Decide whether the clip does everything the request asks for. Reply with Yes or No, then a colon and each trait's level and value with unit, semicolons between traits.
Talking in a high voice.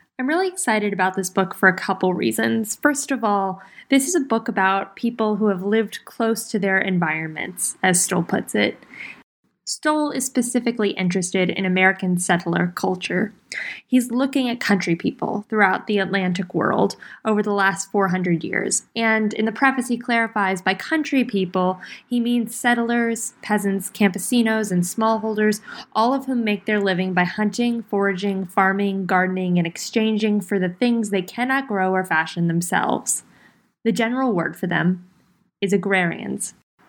Yes: high, 200 Hz